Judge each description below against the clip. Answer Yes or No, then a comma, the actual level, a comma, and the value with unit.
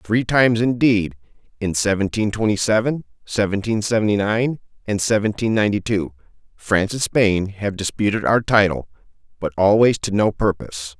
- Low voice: Yes, low, 105 Hz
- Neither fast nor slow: No, slow, 130 wpm